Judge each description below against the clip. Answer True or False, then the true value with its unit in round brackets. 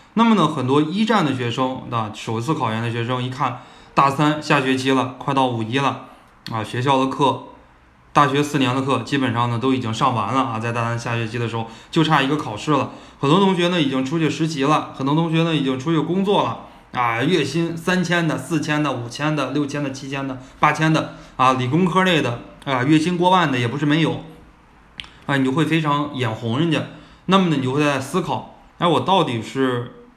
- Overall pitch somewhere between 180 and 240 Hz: False (140 Hz)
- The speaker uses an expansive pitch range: False (3.6 semitones)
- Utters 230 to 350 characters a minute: True (310 characters per minute)